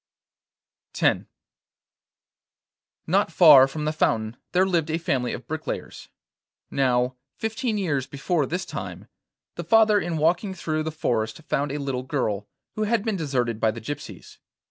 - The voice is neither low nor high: Yes, medium, 150 Hz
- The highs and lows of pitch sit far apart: Yes, wide, 5.9 semitones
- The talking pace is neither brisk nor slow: Yes, average, 145 wpm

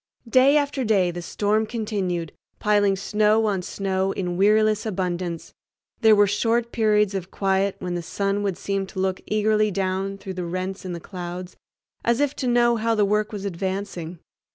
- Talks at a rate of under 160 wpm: No, average, 175 wpm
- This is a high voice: Yes, high, 200 Hz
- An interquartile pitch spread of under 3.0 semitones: Yes, narrow, 2.5 semitones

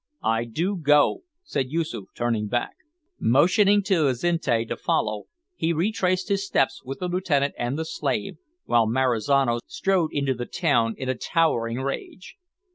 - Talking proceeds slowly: No, average, 150 wpm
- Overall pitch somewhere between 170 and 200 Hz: No, medium, 140 Hz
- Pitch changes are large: Yes, wide, 6.5 semitones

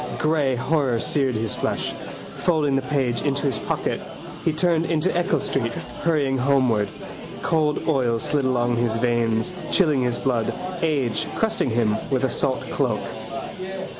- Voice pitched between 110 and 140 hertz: Yes, low, 135 Hz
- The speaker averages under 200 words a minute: Yes, average, 145 wpm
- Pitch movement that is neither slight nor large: Yes, average, 4.2 semitones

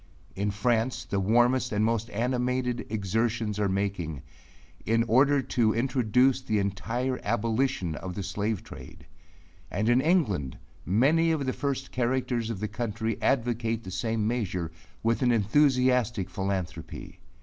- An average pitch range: Yes, average, 3.6 semitones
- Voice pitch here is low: Yes, low, 115 Hz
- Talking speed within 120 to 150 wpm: Yes, average, 140 wpm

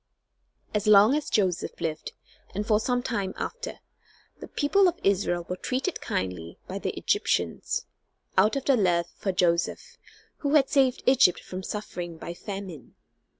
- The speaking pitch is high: Yes, high, 200 Hz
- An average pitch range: No, wide, 6.8 semitones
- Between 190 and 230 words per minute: No, average, 150 wpm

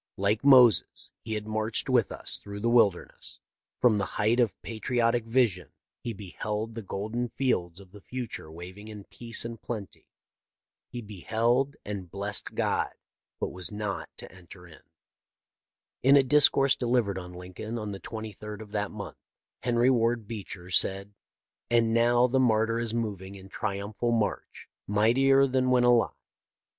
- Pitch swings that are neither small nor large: Yes, average, 3.1 semitones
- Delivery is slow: No, average, 155 wpm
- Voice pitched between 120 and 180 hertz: No, low, 110 Hz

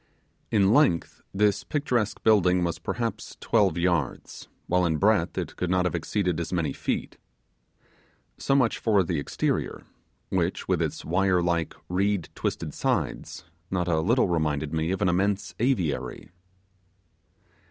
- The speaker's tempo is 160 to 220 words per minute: No, average, 140 wpm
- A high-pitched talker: No, very low, 90 Hz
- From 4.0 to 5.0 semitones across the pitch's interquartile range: No, average, 3.6 semitones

